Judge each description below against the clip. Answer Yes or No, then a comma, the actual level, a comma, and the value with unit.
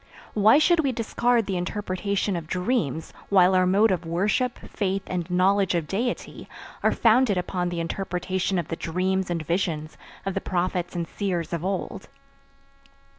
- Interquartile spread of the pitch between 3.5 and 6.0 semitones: No, narrow, 2.6 semitones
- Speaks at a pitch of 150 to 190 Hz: Yes, medium, 185 Hz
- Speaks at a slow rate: No, average, 160 wpm